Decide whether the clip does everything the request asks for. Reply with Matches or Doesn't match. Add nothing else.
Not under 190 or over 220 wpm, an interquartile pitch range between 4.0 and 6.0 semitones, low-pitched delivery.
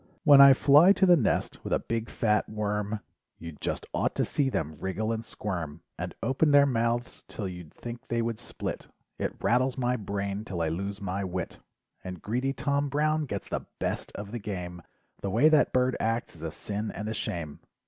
Matches